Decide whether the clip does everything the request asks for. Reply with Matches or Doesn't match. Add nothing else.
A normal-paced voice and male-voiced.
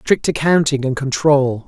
Matches